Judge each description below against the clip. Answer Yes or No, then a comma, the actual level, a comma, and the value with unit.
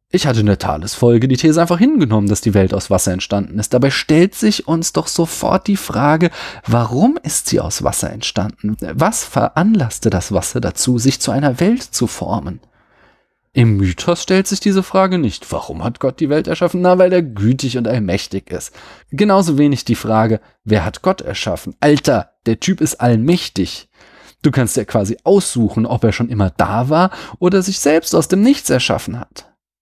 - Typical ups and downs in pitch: No, wide, 8.4 semitones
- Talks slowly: No, fast, 190 wpm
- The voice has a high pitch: No, low, 135 Hz